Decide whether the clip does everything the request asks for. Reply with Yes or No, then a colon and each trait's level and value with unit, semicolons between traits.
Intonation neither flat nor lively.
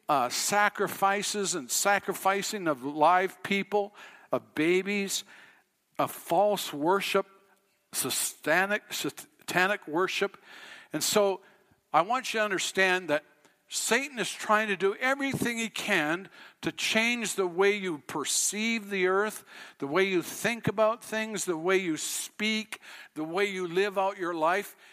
No: narrow, 2.1 semitones